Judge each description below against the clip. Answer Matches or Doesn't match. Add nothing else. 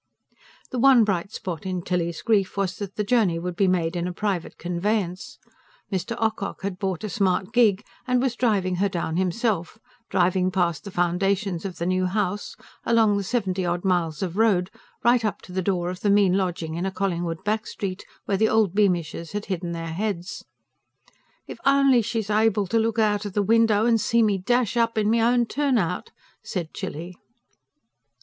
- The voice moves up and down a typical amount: Matches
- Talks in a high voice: Matches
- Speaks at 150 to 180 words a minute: Doesn't match